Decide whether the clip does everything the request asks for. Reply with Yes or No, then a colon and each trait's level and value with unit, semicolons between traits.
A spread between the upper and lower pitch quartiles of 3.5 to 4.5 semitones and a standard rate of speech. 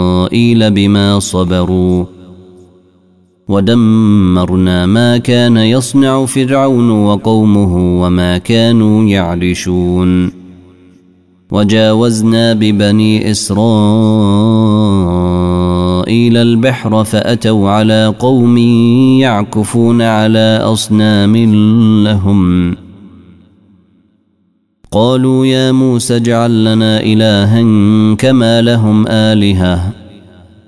No: average, 3.8 semitones; slow, 60 wpm